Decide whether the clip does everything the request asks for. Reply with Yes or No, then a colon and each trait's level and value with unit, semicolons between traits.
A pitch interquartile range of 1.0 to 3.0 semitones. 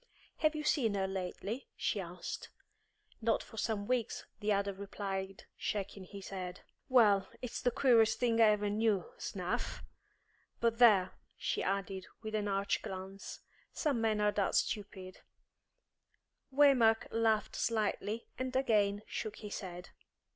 Yes: average, 2.7 semitones